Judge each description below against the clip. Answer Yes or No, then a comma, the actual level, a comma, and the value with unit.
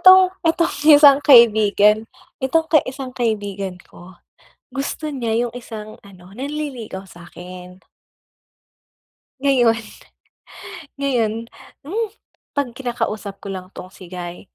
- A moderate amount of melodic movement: No, wide, 6.0 semitones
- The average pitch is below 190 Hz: No, high, 230 Hz